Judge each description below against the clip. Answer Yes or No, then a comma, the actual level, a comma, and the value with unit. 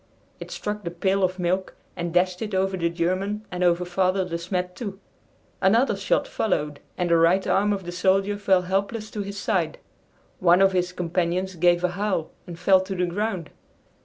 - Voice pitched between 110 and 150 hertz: No, medium, 185 Hz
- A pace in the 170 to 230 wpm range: Yes, average, 190 wpm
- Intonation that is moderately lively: No, narrow, 2.0 semitones